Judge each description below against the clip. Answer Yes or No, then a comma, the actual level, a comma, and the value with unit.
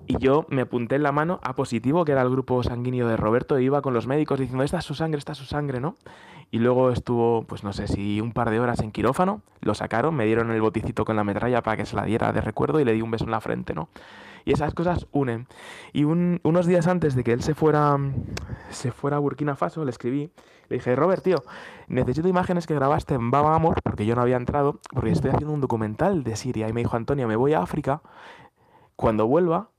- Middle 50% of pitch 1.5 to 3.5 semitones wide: No, average, 4.6 semitones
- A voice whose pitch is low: Yes, low, 130 Hz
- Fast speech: Yes, fast, 250 wpm